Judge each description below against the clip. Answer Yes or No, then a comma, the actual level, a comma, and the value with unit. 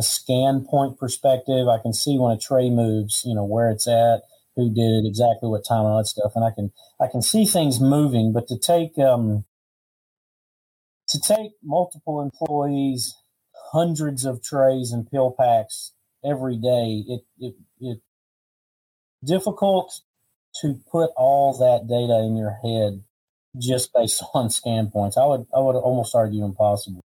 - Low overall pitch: Yes, low, 125 Hz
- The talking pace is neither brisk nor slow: Yes, average, 160 wpm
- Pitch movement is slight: No, average, 3.7 semitones